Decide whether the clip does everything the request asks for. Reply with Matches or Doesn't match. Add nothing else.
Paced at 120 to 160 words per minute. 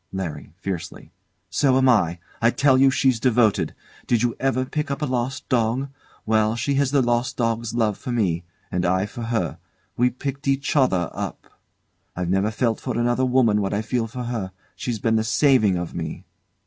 Doesn't match